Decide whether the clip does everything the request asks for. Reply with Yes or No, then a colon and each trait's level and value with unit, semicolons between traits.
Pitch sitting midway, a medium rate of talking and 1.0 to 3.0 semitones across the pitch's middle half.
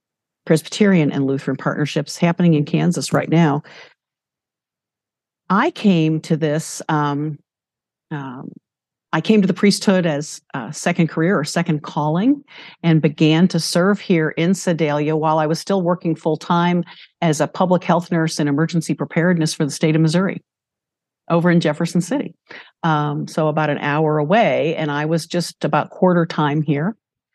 Yes: medium, 160 Hz; average, 160 wpm; narrow, 2.5 semitones